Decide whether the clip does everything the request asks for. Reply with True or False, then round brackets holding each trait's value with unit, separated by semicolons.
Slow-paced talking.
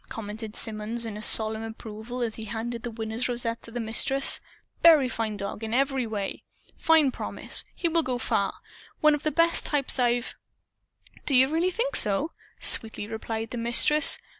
False (170 wpm)